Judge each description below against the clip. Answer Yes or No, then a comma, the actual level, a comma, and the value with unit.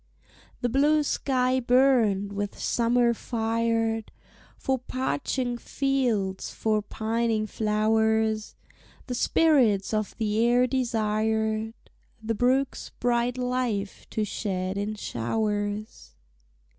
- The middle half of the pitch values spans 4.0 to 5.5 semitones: No, average, 2.7 semitones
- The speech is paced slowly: Yes, slow, 95 wpm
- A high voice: Yes, high, 225 Hz